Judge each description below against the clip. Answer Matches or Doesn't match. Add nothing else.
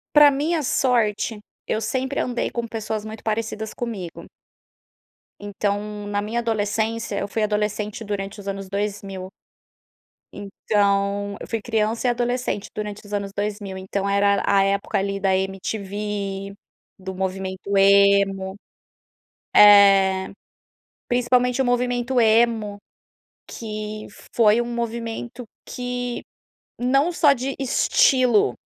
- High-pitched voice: Matches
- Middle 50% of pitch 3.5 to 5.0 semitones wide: Doesn't match